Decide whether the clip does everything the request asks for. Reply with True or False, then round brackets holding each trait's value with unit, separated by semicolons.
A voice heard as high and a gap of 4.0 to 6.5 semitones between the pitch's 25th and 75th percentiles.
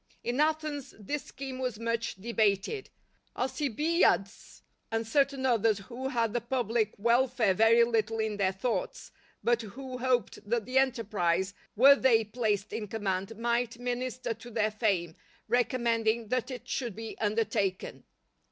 False (230 Hz; 2.9 semitones)